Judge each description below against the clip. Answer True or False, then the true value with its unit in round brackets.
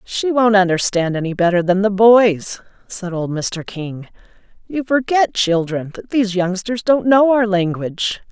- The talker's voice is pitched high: True (200 Hz)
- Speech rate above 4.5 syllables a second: False (4.4 syllables/s)